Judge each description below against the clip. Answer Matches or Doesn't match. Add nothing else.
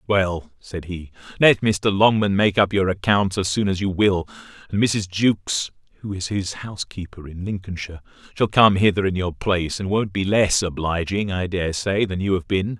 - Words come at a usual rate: Matches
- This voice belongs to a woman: Doesn't match